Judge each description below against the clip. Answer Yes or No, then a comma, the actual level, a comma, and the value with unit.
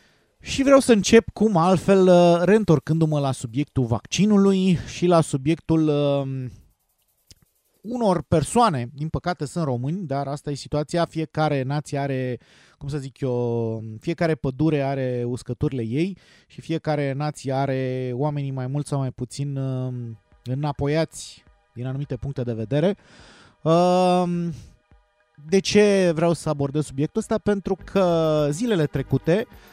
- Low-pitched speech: No, medium, 150 Hz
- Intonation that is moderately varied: Yes, average, 4.5 semitones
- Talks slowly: No, average, 135 wpm